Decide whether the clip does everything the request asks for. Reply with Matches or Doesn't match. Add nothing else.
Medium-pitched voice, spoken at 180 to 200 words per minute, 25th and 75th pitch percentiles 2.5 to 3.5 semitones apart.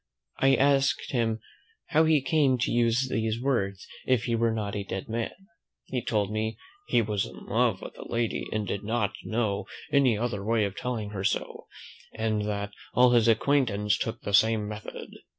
Doesn't match